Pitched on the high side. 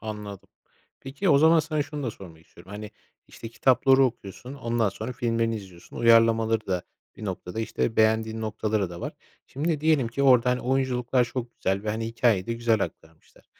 No: low, 115 Hz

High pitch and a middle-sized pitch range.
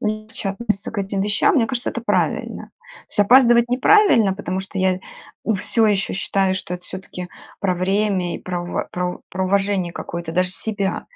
Yes: high, 195 Hz; average, 3.0 semitones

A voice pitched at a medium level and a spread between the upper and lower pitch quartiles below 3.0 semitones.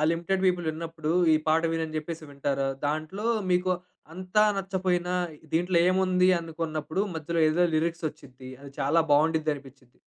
Yes: medium, 165 Hz; narrow, 2.6 semitones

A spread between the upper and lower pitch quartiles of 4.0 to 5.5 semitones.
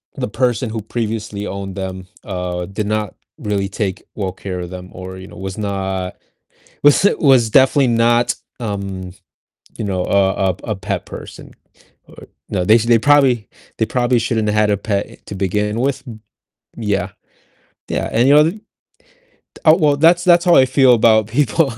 Yes: average, 4.3 semitones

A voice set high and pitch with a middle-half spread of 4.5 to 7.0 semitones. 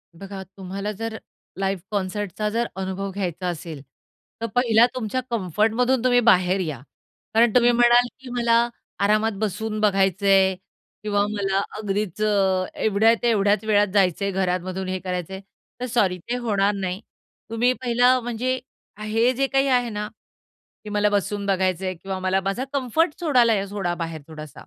No: high, 205 Hz; average, 3.6 semitones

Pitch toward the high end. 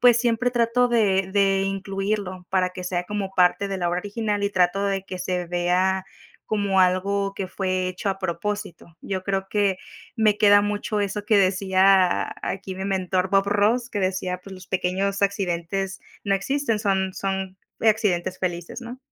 Yes: high, 195 Hz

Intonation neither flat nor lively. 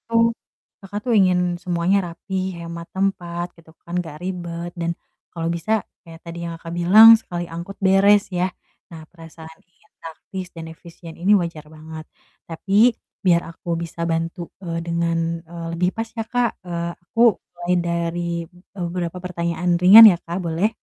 No: narrow, 1.8 semitones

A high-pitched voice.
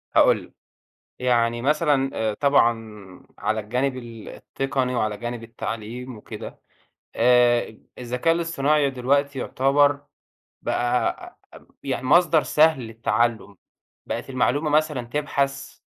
No: low, 125 Hz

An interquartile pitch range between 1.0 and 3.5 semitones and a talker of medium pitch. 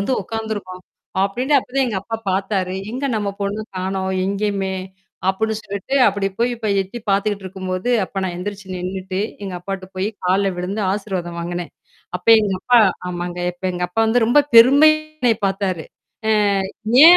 No: average, 3.0 semitones; high, 195 Hz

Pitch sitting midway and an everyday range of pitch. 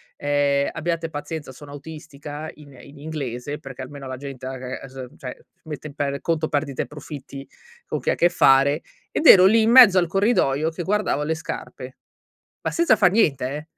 Yes: medium, 145 Hz; average, 3.0 semitones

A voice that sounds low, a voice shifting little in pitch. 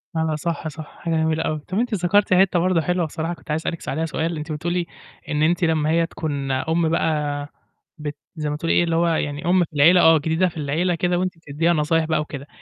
No: medium, 160 Hz; narrow, 2.2 semitones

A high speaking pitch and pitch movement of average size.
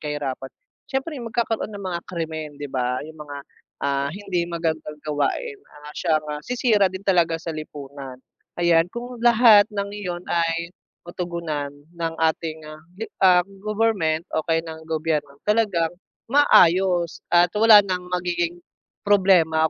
No: medium, 170 Hz; average, 4.2 semitones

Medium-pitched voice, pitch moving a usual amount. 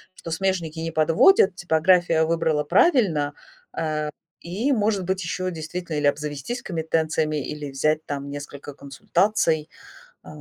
Yes: medium, 160 Hz; average, 3.2 semitones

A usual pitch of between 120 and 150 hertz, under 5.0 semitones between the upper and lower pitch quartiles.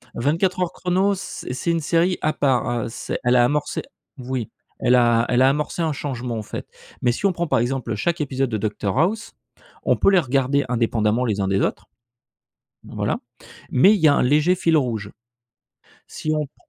No: low, 135 Hz; wide, 5.4 semitones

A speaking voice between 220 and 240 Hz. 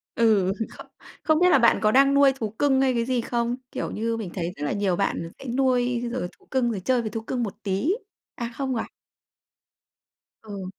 Yes: high, 235 Hz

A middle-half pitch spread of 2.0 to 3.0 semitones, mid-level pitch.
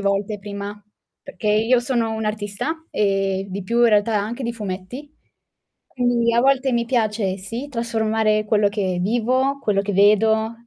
No: average, 2.7 semitones; high, 220 Hz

